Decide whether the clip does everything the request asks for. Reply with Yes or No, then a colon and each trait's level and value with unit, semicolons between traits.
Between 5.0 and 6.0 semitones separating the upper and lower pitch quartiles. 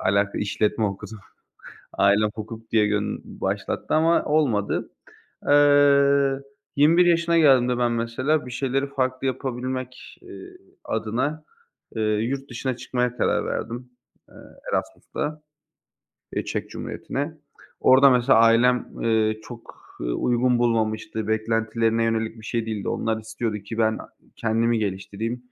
No: average, 3.4 semitones